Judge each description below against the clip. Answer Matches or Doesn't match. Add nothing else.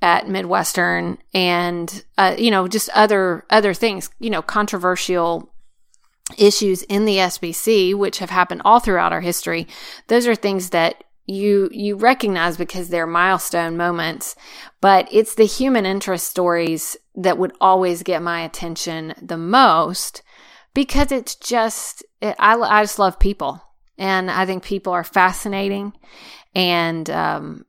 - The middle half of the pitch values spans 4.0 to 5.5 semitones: Doesn't match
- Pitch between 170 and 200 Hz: Matches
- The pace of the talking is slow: Doesn't match